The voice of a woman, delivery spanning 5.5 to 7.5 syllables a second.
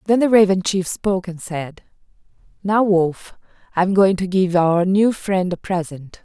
No: female; 4.5 syllables/s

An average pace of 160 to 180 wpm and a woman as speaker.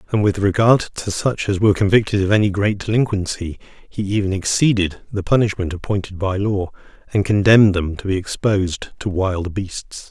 No: average, 170 wpm; male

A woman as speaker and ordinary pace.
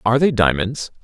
No: male; average, 175 wpm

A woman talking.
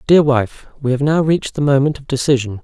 No: male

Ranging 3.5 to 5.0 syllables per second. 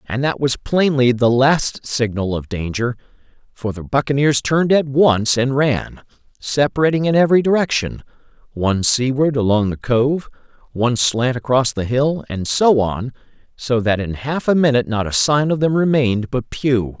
Yes: 4.8 syllables/s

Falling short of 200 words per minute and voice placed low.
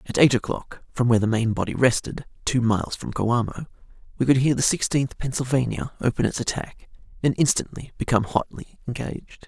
Yes: average, 170 wpm; low, 125 Hz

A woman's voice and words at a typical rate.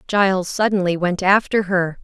Yes: female; average, 145 wpm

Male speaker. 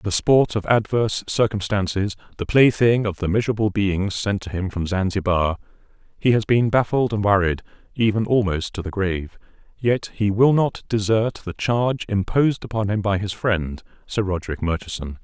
Yes: male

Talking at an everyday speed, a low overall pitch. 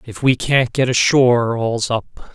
Yes: average, 180 wpm; low, 120 Hz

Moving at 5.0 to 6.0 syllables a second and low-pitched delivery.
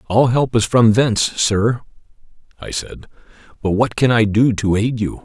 No: 4.6 syllables/s; low, 110 Hz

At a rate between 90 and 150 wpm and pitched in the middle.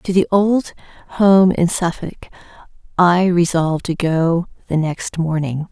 Yes: slow, 135 wpm; medium, 175 Hz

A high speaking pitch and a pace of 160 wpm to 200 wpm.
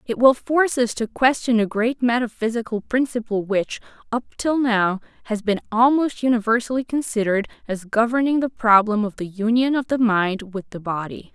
Yes: high, 230 Hz; average, 170 wpm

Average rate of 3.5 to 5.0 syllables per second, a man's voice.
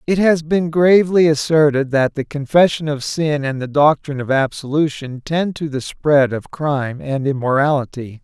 Yes: 4.8 syllables/s; male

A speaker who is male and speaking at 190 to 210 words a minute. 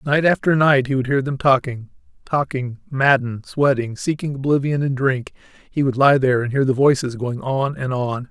Yes: male; average, 195 wpm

